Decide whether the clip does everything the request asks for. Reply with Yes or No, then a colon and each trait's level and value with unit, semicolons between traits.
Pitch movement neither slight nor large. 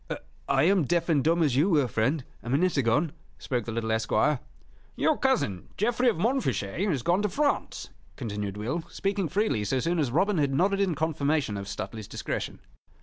No: wide, 7.9 semitones